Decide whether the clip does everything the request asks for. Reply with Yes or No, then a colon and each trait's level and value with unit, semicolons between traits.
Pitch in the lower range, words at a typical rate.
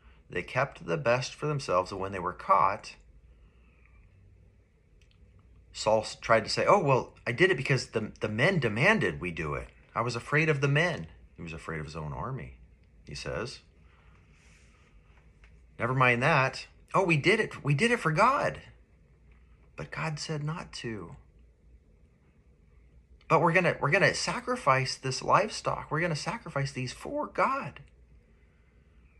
Yes: very low, 85 Hz; average, 150 wpm